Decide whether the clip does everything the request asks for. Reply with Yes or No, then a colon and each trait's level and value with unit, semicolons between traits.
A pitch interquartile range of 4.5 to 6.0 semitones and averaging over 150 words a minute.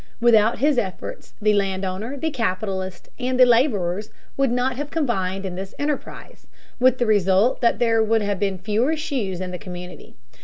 Yes: average, 4.9 semitones; average, 180 wpm